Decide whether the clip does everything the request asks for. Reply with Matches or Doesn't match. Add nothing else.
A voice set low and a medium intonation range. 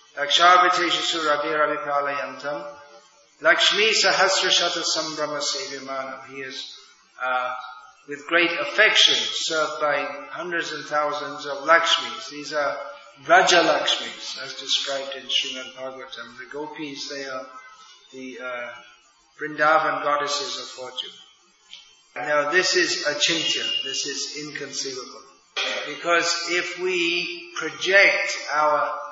Doesn't match